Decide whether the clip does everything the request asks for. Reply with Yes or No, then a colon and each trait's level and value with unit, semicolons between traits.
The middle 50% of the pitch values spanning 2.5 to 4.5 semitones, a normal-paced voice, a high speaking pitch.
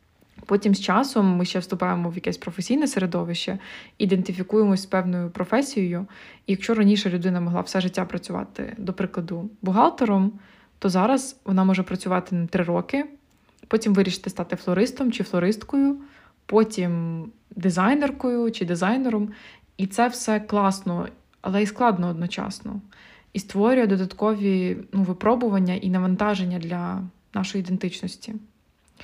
Yes: average, 2.9 semitones; average, 125 wpm; high, 195 Hz